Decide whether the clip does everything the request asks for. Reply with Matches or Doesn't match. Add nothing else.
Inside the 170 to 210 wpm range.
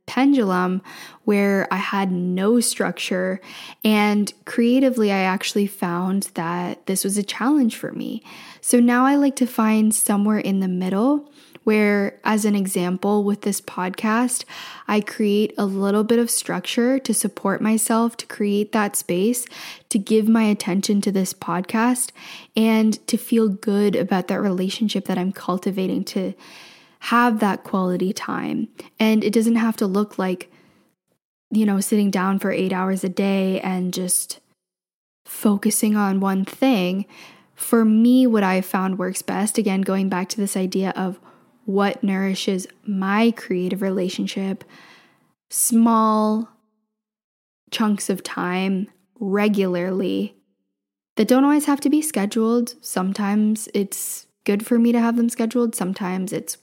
Doesn't match